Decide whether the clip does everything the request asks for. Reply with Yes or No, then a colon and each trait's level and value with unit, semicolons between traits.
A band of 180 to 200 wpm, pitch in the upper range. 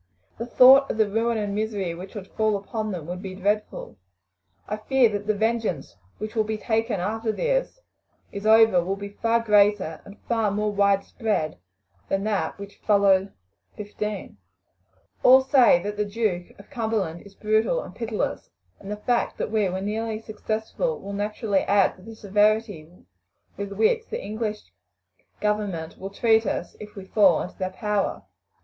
No: average, 165 wpm; high, 210 Hz